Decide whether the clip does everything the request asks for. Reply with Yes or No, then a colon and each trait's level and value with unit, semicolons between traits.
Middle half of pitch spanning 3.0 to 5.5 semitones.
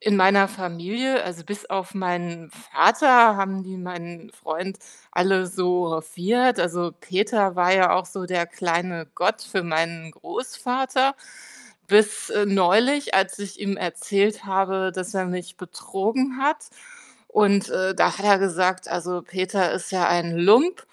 No: narrow, 2.4 semitones